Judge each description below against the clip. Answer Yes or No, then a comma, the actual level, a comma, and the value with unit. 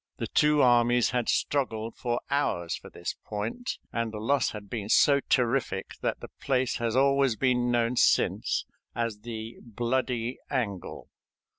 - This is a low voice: Yes, low, 120 Hz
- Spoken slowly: No, average, 150 wpm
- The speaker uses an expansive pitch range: No, average, 2.7 semitones